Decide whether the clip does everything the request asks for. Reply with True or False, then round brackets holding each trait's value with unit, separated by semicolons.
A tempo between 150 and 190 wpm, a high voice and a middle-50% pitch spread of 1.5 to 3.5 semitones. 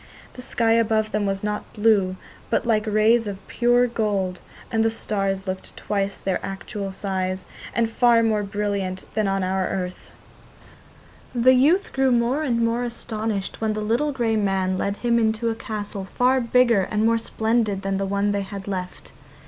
True (175 wpm; 215 Hz; 2.9 semitones)